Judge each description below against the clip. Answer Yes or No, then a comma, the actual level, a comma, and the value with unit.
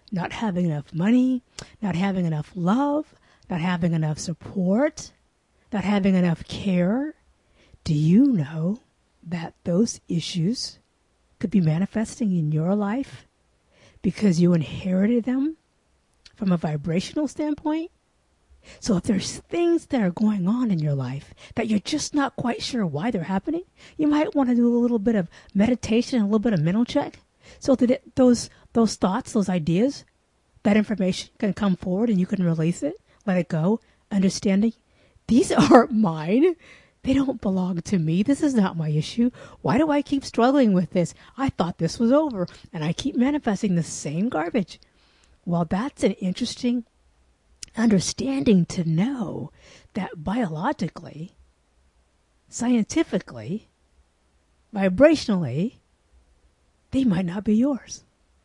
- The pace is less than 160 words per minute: Yes, average, 145 wpm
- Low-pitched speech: No, high, 200 Hz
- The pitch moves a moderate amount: No, wide, 6.2 semitones